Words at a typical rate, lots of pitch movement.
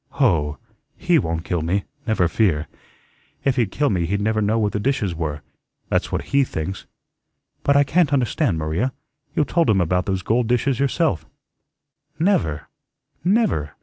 Yes: average, 160 wpm; wide, 8.5 semitones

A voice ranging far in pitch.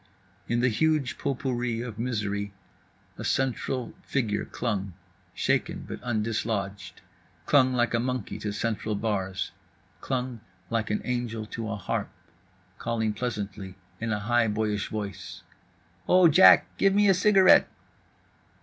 No: average, 3.2 semitones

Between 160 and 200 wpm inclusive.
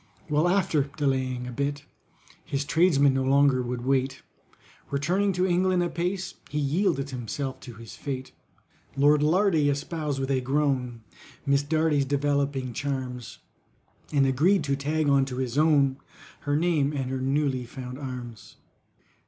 No: average, 145 wpm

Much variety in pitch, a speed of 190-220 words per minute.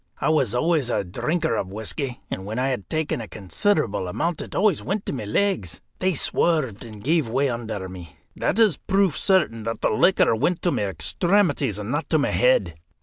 Yes: wide, 8.3 semitones; fast, 205 wpm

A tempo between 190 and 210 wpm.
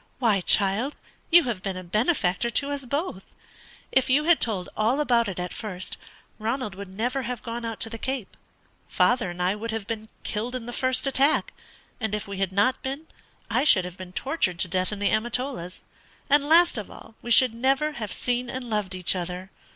Yes: fast, 205 wpm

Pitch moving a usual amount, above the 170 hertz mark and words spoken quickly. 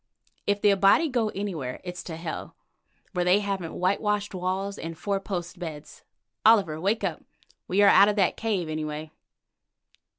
No: average, 3.3 semitones; high, 190 Hz; average, 160 wpm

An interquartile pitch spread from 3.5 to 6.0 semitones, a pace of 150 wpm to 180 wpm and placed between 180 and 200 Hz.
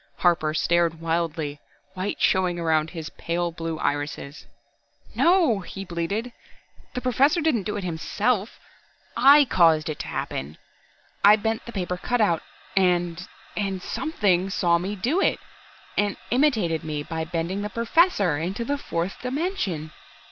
No: wide, 5.5 semitones; average, 140 wpm; medium, 185 Hz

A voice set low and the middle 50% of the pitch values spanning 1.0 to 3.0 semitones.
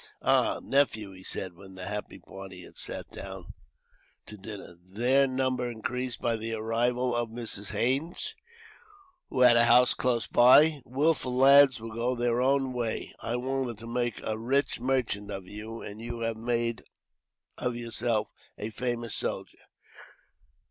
Yes: low, 120 Hz; narrow, 2.5 semitones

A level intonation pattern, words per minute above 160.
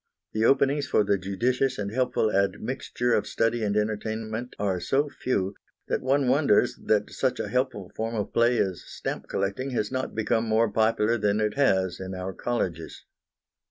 No: average, 3.9 semitones; average, 170 wpm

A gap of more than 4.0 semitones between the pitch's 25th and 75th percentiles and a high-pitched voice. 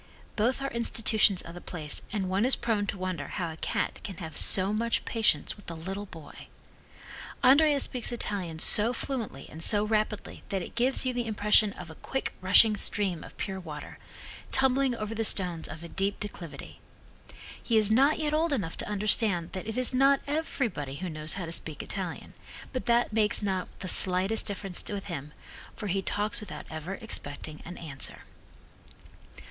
Yes: average, 4.7 semitones; high, 205 Hz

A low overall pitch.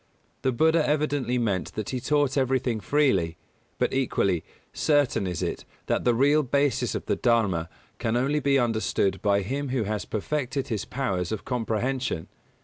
Yes: low, 125 Hz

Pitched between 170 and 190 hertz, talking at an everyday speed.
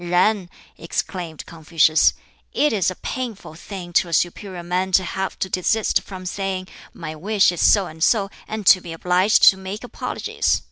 Yes: medium, 185 Hz; average, 175 wpm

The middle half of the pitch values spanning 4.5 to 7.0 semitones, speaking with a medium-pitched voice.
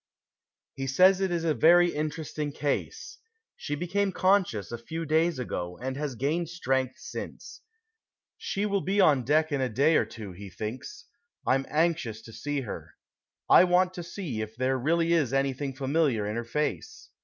Yes: average, 5.1 semitones; medium, 150 Hz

